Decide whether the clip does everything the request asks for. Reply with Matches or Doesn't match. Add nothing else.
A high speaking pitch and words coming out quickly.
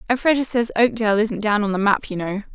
Matches